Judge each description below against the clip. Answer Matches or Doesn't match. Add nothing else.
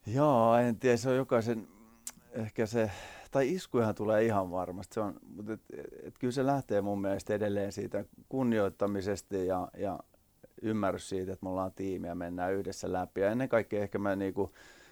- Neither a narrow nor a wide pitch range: Matches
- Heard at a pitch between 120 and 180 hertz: Doesn't match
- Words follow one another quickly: Matches